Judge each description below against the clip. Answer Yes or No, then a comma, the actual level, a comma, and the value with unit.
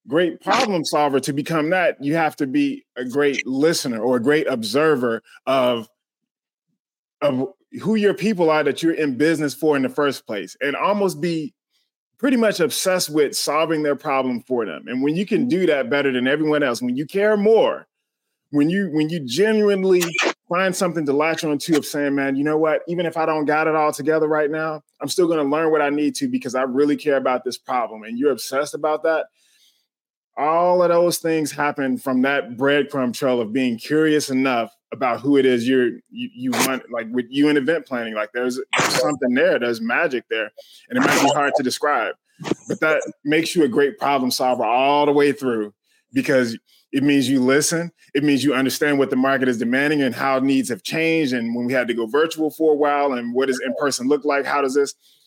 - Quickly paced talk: Yes, fast, 215 wpm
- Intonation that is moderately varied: Yes, average, 3.4 semitones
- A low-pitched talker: No, medium, 145 Hz